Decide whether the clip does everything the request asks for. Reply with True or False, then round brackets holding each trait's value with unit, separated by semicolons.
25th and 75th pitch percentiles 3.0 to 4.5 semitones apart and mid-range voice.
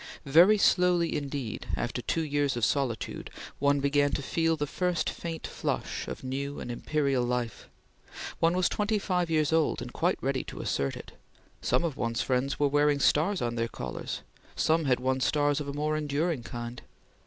True (3.9 semitones; 145 Hz)